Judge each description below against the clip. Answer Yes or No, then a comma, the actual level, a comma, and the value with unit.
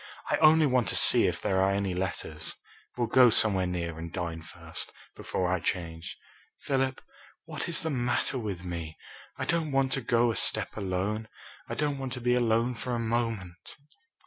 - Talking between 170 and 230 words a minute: Yes, average, 185 wpm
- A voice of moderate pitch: No, low, 110 Hz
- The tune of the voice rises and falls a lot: Yes, wide, 5.8 semitones